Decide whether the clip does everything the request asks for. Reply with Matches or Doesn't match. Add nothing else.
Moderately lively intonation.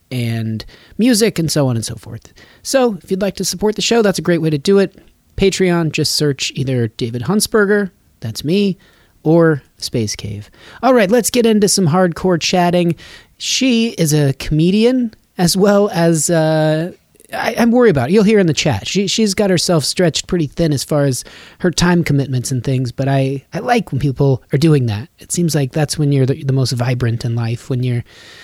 Doesn't match